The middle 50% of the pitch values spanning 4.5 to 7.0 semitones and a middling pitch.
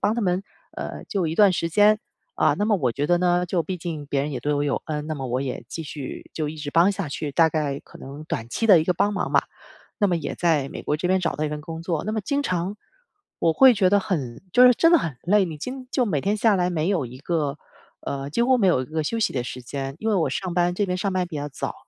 Yes: average, 5.1 semitones; medium, 170 Hz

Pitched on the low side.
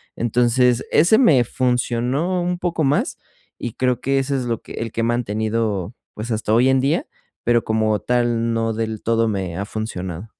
Yes: low, 120 Hz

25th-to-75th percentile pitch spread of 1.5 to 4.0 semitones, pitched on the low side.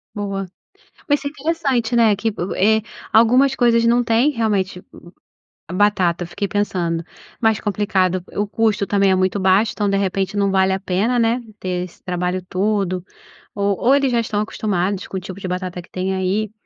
No: average, 3.3 semitones; high, 200 Hz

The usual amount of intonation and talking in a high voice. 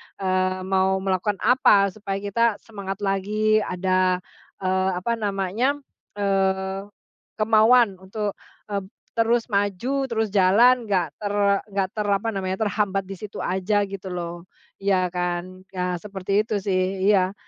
No: narrow, 2.0 semitones; high, 195 Hz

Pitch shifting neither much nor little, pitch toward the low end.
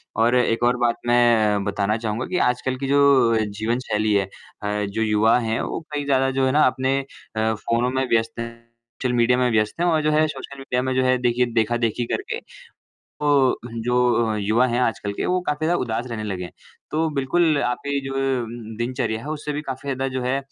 Yes: average, 3.2 semitones; low, 125 Hz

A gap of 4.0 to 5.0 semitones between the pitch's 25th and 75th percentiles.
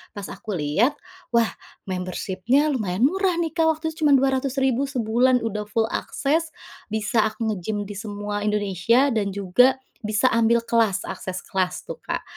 Yes: average, 4.6 semitones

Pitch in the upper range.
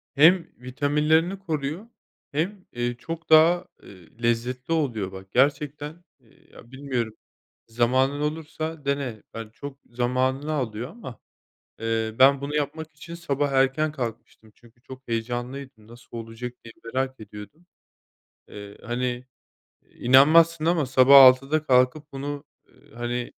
No: low, 135 Hz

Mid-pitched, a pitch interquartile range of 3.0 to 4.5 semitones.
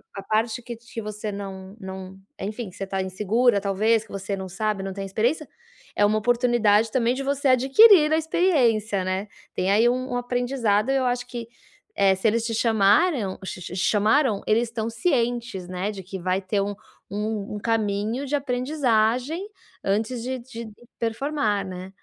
No: high, 220 Hz; average, 3.8 semitones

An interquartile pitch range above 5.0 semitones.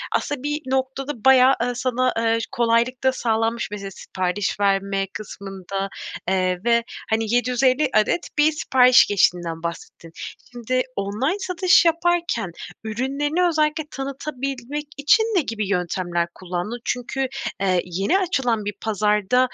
Yes: wide, 5.5 semitones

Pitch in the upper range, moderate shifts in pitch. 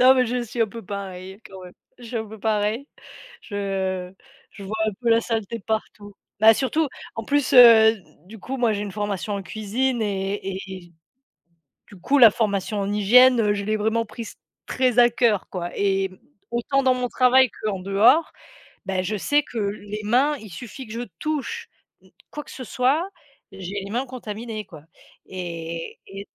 Yes: high, 215 Hz; average, 3.7 semitones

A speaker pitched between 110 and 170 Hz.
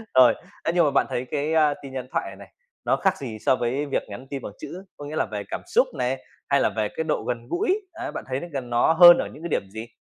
Yes: low, 135 Hz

